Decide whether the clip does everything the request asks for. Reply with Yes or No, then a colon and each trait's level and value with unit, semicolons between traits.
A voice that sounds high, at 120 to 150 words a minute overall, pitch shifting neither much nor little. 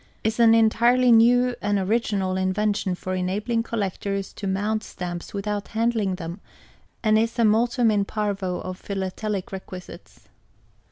Yes: high, 210 Hz; average, 145 wpm; average, 3.1 semitones